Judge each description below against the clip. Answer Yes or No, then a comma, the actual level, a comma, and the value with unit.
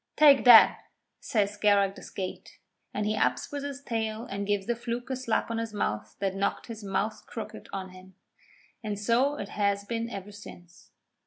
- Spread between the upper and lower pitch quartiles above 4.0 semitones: No, average, 2.9 semitones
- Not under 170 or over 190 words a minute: Yes, average, 185 wpm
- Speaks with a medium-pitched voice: No, high, 210 Hz